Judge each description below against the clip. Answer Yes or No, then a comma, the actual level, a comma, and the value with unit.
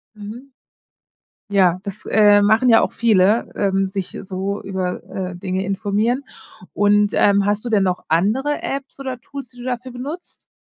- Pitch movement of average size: Yes, average, 4.0 semitones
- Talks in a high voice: Yes, high, 205 Hz